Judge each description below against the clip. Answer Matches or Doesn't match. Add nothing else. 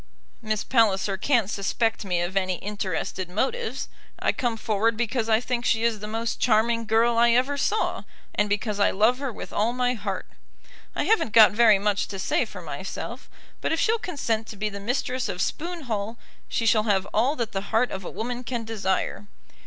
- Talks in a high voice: Matches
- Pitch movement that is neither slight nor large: Matches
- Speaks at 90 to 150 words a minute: Doesn't match